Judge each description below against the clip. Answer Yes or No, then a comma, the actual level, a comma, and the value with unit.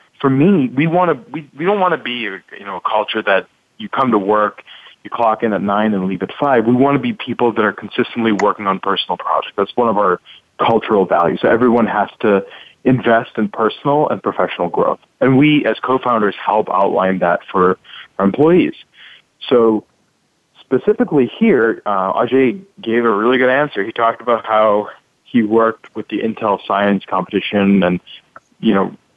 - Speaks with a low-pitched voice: Yes, low, 115 Hz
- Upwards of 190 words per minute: No, average, 185 wpm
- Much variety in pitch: No, average, 4.0 semitones